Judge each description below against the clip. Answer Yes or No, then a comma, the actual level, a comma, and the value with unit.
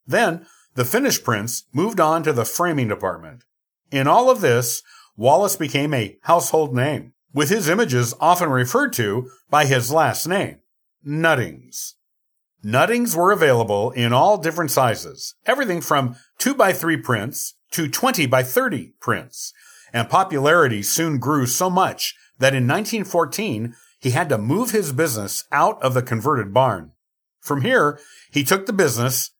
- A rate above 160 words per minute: No, average, 145 wpm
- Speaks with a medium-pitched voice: Yes, medium, 145 Hz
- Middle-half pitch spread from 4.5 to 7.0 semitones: Yes, average, 5.3 semitones